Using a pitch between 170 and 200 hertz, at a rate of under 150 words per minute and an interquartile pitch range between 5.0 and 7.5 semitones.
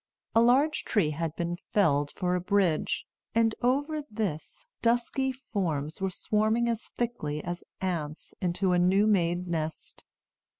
Yes: high, 190 Hz; average, 140 wpm; average, 5.3 semitones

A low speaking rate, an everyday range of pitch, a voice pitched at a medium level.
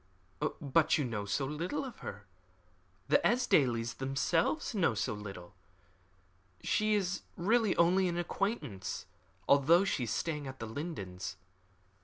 No: slow, 130 wpm; wide, 8.3 semitones; medium, 150 Hz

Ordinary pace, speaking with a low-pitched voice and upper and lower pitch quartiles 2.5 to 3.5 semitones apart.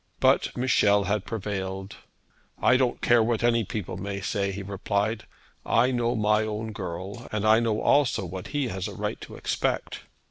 Yes: average, 175 wpm; low, 105 Hz; average, 2.9 semitones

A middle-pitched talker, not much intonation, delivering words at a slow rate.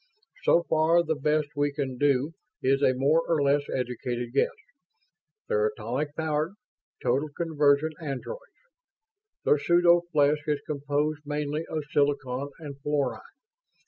Yes: medium, 145 Hz; narrow, 2.0 semitones; slow, 130 wpm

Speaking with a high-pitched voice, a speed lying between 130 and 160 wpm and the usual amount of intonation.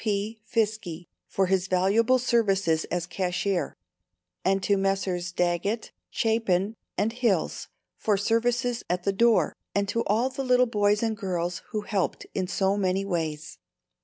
Yes: high, 200 Hz; average, 145 wpm; average, 3.7 semitones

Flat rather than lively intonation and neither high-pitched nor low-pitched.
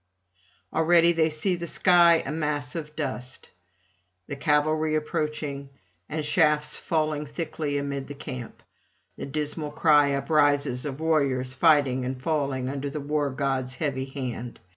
Yes: narrow, 2.1 semitones; medium, 145 Hz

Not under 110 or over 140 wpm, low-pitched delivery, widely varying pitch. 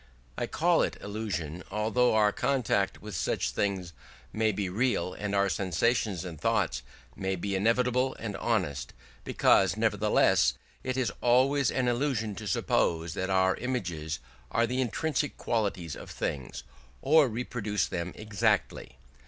No: slow, 135 wpm; low, 105 Hz; average, 4.8 semitones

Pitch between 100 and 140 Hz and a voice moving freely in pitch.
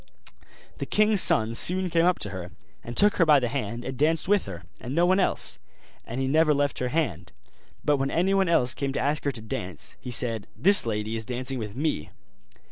Yes: low, 135 Hz; wide, 6.4 semitones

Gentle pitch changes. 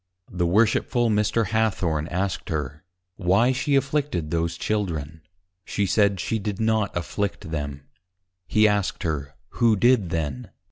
No: average, 5.1 semitones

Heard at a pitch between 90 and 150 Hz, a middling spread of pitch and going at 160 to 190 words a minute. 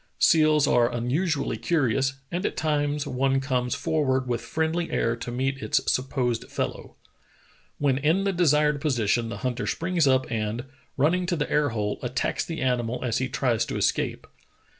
Yes: low, 135 Hz; average, 3.9 semitones; average, 165 wpm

